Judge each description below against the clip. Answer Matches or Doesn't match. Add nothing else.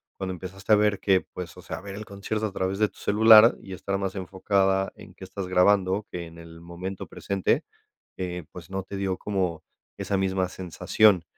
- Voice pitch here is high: Doesn't match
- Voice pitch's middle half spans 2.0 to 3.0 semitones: Doesn't match